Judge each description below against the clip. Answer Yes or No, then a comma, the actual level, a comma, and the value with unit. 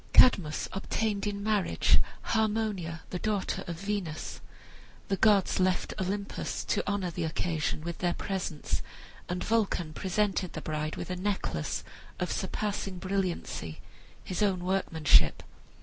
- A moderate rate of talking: No, slow, 130 wpm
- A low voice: No, medium, 185 Hz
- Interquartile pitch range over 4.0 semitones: No, average, 3.3 semitones